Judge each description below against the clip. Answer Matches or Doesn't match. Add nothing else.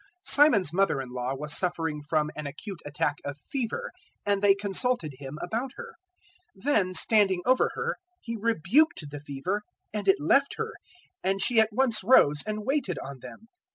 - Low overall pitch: Doesn't match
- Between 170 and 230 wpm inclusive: Matches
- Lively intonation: Matches